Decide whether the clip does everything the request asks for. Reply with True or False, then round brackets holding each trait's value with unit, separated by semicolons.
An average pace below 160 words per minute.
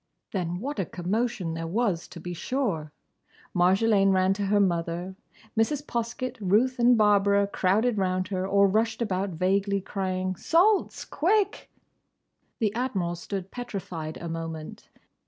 True (140 wpm)